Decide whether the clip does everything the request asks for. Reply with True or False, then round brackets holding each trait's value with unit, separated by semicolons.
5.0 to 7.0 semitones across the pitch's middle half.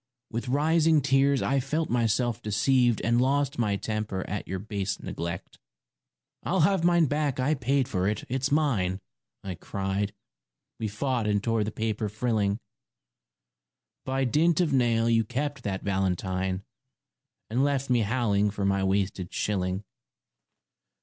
True (5.3 semitones)